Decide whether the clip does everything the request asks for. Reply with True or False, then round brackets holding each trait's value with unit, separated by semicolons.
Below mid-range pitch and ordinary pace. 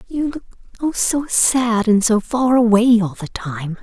False (230 Hz; 190 wpm)